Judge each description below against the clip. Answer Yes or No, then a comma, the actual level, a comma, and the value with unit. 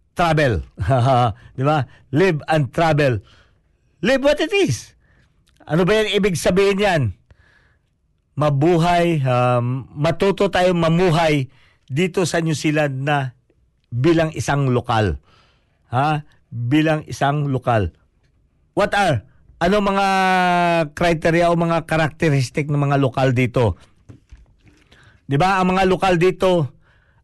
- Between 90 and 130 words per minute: Yes, slow, 110 wpm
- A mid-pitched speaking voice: Yes, medium, 150 Hz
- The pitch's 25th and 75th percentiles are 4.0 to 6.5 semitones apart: Yes, wide, 5.6 semitones